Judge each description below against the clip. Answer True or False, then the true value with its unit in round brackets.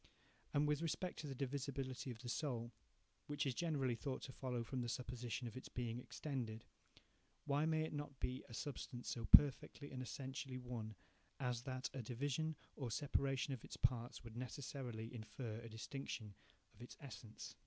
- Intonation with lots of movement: False (2.9 semitones)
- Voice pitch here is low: True (130 Hz)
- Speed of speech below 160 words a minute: False (175 wpm)